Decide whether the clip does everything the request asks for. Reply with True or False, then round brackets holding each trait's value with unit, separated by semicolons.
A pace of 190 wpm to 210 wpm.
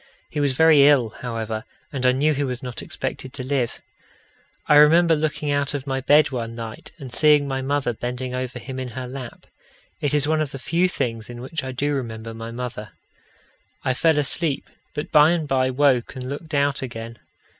True (200 wpm)